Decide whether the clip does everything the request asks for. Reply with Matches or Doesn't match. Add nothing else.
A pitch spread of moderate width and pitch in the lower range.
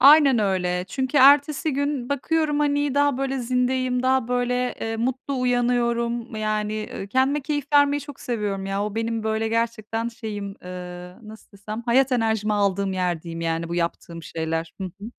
Doesn't match